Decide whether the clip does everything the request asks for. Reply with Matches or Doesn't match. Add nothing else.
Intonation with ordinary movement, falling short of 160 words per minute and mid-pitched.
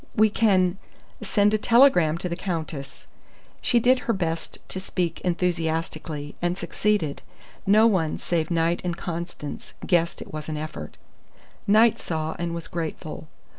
Matches